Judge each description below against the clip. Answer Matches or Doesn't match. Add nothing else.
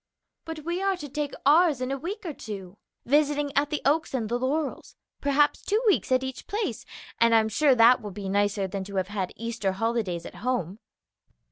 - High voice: Matches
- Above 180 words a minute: Matches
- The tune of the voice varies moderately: Doesn't match